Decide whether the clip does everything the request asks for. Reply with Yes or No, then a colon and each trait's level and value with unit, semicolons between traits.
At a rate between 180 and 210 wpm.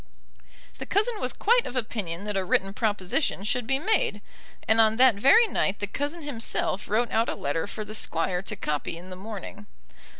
Yes: average, 195 wpm